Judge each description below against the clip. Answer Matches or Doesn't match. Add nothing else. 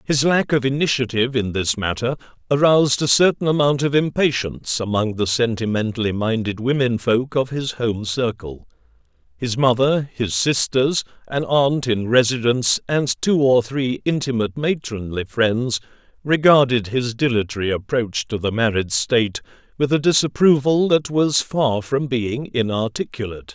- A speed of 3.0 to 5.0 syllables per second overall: Matches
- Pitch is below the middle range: Matches